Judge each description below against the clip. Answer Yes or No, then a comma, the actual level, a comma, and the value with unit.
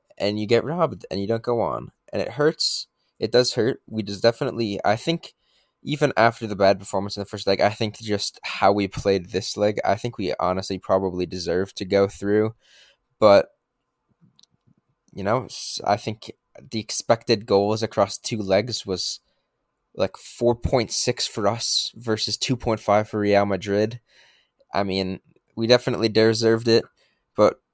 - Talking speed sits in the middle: Yes, average, 160 wpm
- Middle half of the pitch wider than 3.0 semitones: No, narrow, 2.6 semitones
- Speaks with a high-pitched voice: No, low, 105 Hz